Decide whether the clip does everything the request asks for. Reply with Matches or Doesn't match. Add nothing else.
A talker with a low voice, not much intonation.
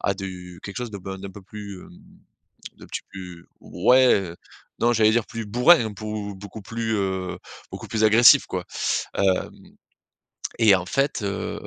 Doesn't match